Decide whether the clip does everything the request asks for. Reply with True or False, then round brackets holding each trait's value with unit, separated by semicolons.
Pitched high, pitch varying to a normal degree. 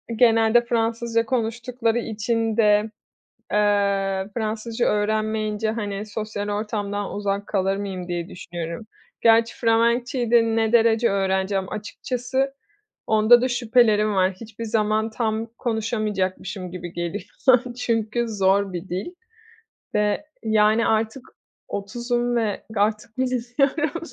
False (220 Hz; 2.3 semitones)